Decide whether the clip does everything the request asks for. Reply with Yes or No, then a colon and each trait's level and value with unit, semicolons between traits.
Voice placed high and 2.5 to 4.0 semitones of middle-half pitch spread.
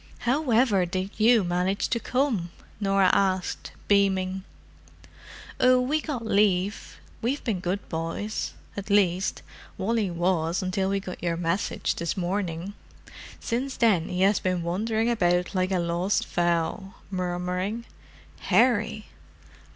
Yes: high, 195 Hz; average, 3.5 semitones